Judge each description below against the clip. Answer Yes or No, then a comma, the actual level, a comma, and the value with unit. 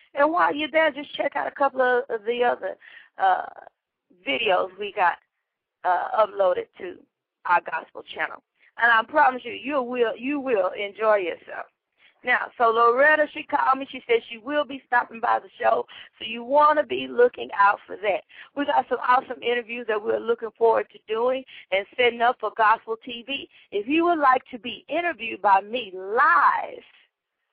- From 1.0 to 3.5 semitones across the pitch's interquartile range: No, average, 4.5 semitones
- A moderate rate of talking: Yes, average, 180 wpm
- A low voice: No, very high, 255 Hz